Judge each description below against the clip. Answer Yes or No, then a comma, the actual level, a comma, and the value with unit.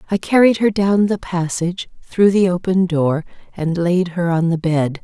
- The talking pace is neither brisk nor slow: Yes, average, 190 wpm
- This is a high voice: No, medium, 180 Hz